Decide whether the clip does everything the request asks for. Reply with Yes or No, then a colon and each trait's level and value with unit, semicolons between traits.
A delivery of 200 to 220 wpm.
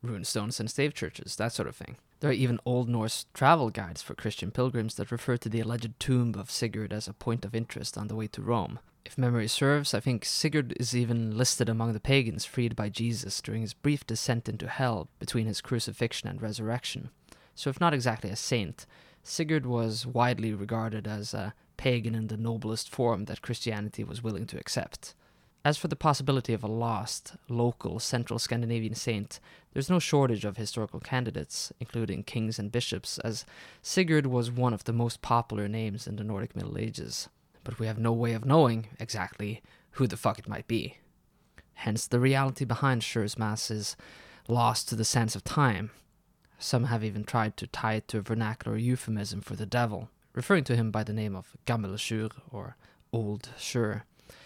No: average, 190 wpm